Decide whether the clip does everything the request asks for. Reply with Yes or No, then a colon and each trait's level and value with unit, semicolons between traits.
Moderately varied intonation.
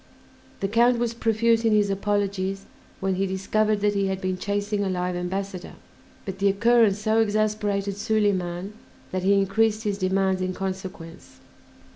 No: narrow, 2.1 semitones